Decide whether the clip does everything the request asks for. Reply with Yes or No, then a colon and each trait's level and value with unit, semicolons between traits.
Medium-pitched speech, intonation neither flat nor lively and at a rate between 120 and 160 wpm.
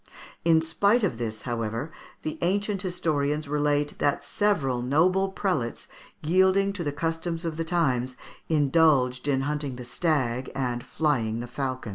Yes: medium, 150 Hz; average, 5.0 semitones; average, 145 wpm